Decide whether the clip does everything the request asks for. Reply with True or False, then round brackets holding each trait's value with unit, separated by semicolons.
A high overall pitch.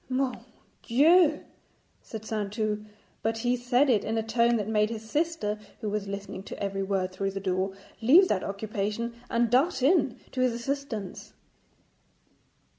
True (225 Hz)